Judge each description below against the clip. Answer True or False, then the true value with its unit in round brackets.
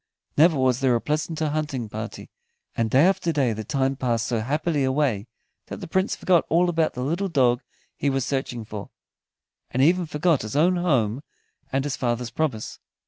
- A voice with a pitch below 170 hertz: True (135 Hz)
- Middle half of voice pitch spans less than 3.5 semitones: False (4.8 semitones)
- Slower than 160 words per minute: False (185 wpm)